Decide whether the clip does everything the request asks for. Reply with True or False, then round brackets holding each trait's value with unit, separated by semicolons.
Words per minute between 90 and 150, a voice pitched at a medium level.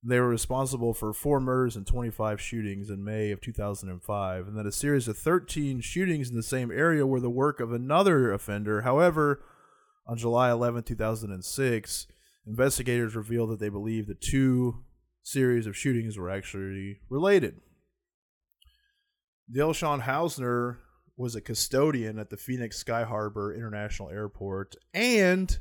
False (145 wpm; 120 Hz)